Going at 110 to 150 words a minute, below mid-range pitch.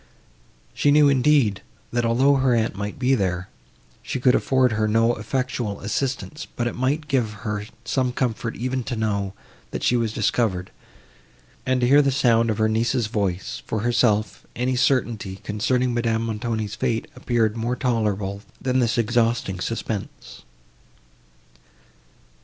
Yes: average, 145 wpm; low, 115 Hz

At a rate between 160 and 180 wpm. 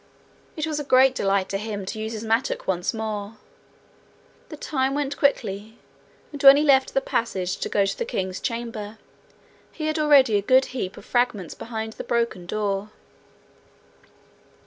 Yes: average, 170 wpm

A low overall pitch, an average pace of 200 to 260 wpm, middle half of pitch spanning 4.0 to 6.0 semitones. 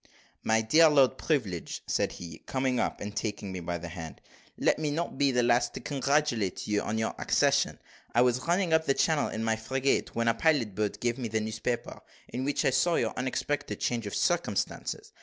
Yes: low, 120 Hz; fast, 205 wpm; average, 4.7 semitones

